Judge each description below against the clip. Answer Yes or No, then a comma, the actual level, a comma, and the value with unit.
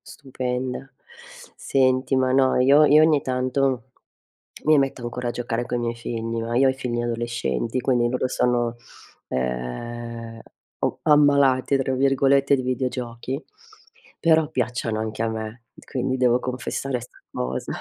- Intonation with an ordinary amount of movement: No, narrow, 2.3 semitones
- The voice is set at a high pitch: No, low, 125 Hz